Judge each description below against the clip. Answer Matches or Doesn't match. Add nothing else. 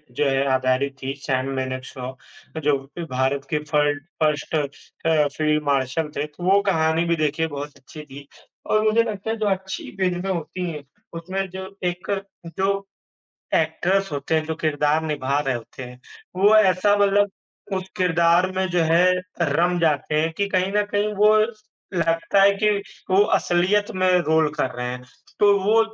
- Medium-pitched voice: Matches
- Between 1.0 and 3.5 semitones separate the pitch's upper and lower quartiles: Doesn't match